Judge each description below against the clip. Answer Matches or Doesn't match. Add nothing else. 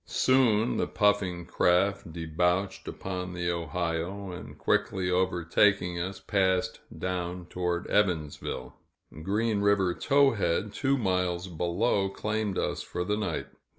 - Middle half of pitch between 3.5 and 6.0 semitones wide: Doesn't match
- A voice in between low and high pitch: Doesn't match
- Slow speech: Matches